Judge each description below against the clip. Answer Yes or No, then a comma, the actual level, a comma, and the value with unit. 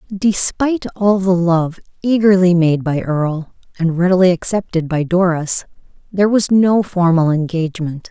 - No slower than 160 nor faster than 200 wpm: No, slow, 135 wpm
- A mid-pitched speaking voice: Yes, medium, 180 Hz